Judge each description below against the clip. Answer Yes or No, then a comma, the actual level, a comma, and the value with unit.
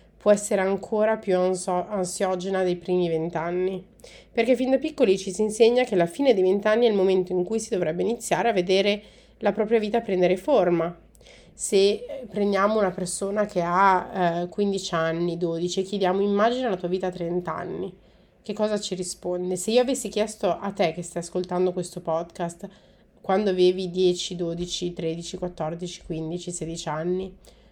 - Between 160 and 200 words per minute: Yes, average, 165 wpm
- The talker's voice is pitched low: No, medium, 185 Hz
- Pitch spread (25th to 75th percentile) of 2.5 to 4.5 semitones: Yes, average, 2.8 semitones